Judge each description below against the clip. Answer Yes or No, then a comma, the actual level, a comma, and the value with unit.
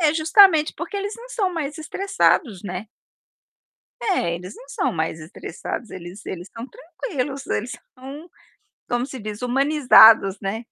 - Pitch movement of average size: No, wide, 8.0 semitones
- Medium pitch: No, very high, 260 Hz